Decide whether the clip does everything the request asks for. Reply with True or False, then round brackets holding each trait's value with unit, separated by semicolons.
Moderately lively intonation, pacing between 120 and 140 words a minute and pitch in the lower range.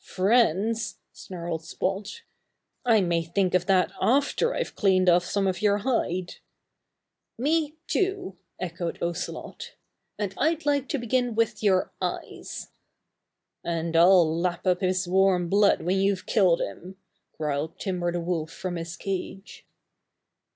False (3.9 semitones; 135 wpm; 185 Hz)